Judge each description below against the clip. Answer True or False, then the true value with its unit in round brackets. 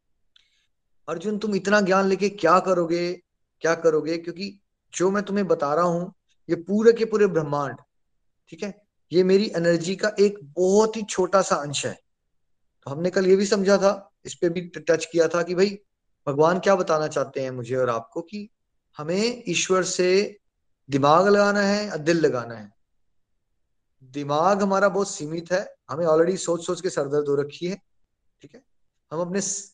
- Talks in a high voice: False (175 Hz)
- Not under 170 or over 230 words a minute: True (175 wpm)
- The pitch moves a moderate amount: True (4.6 semitones)